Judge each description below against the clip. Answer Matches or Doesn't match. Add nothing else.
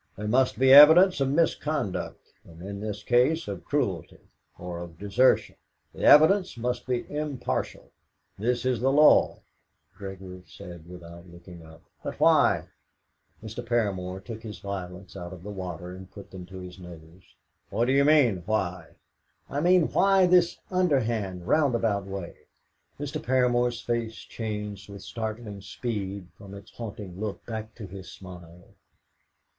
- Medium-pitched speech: Doesn't match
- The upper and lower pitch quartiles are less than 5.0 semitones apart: Doesn't match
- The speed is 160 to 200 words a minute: Doesn't match